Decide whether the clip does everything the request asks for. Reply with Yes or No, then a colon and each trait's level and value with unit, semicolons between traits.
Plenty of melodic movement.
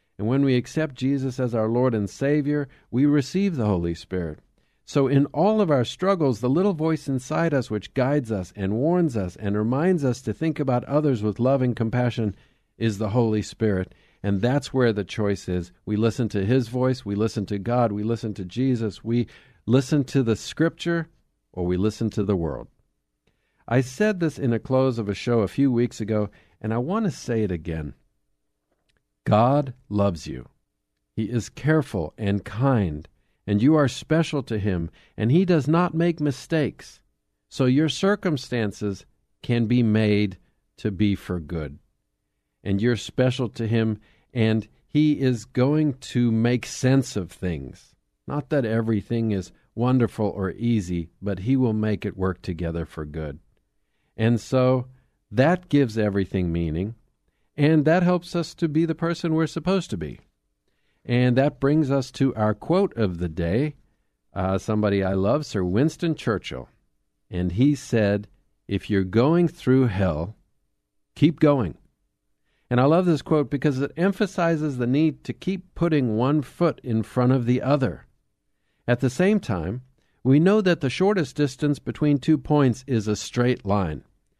Yes: wide, 6.0 semitones